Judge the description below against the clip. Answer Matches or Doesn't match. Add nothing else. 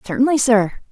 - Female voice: Matches